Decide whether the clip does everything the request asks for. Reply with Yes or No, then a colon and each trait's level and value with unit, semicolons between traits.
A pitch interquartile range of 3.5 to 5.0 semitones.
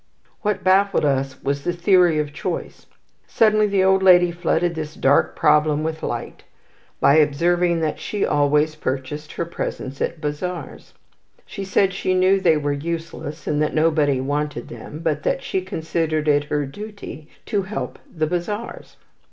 Yes: average, 3.8 semitones